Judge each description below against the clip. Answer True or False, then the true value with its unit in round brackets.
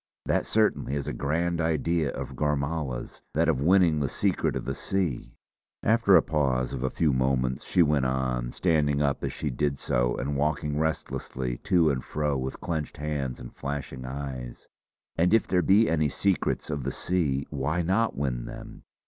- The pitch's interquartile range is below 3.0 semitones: False (3.8 semitones)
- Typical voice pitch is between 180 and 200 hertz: False (75 Hz)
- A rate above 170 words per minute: True (180 wpm)